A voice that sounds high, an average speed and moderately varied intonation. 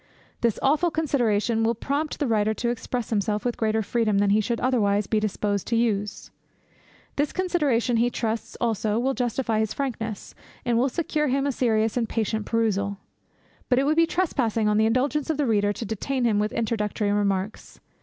Yes: high, 230 Hz; average, 185 wpm; average, 3.6 semitones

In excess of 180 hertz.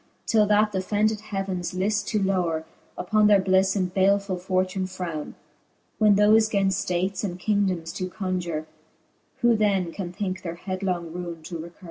Yes: high, 190 Hz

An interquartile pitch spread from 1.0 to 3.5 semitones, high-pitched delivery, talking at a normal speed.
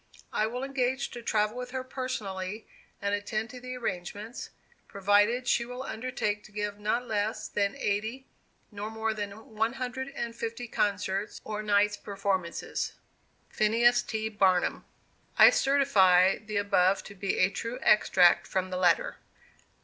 Yes: average, 3.1 semitones; high, 215 Hz; average, 150 wpm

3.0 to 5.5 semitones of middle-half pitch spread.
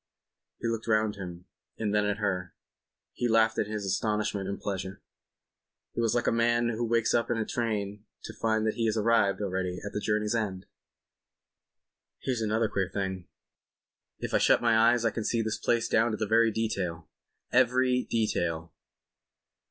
No: narrow, 2.5 semitones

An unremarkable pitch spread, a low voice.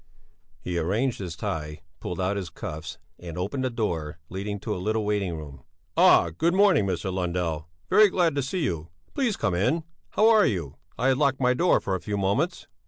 No: wide, 7.6 semitones; low, 100 Hz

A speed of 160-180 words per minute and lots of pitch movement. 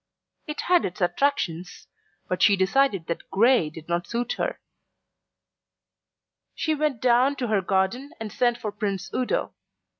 No: average, 145 wpm; wide, 6.1 semitones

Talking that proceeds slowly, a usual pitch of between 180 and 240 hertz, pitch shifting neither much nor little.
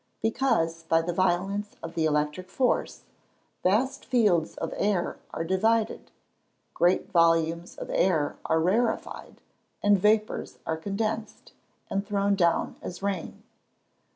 Yes: slow, 125 wpm; high, 190 Hz; average, 4.2 semitones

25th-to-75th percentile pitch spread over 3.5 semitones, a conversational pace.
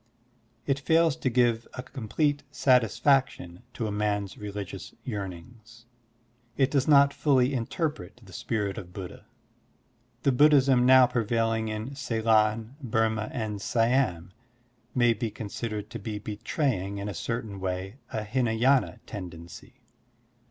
No: average, 3.9 semitones; slow, 125 wpm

